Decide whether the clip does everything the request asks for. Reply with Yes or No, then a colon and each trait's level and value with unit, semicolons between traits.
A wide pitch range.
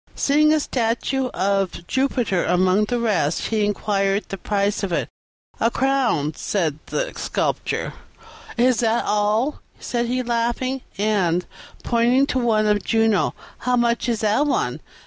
No: average, 3.9 semitones